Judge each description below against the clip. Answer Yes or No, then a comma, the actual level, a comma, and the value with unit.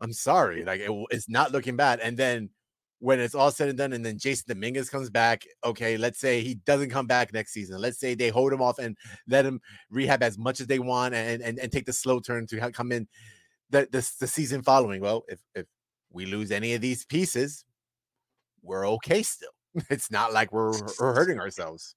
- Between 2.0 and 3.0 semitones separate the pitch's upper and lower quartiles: Yes, narrow, 2.6 semitones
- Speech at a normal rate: No, fast, 220 wpm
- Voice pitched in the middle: No, low, 125 Hz